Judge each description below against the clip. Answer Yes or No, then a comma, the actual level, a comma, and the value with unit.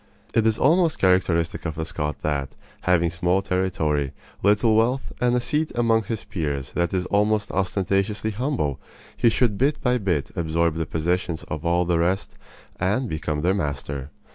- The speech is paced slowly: No, average, 165 wpm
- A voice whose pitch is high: No, very low, 90 Hz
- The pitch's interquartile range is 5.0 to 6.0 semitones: Yes, wide, 5.4 semitones